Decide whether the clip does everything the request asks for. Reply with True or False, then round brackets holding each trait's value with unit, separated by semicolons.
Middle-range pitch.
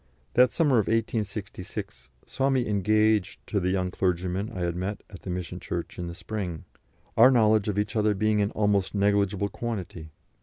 False (100 Hz)